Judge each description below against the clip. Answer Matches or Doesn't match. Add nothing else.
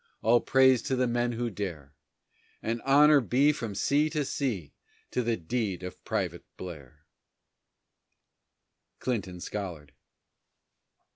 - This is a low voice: Matches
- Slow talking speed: Matches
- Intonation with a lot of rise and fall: Matches